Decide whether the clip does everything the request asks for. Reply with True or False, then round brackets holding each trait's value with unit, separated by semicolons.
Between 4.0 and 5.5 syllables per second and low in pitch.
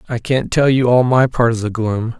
True (5.0 syllables/s; 120 Hz)